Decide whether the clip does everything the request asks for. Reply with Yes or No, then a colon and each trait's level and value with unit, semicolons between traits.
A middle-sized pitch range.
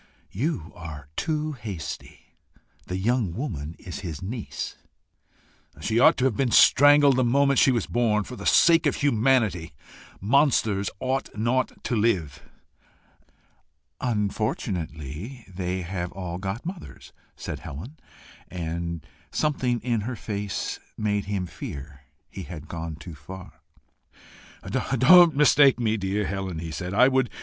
No: wide, 6.6 semitones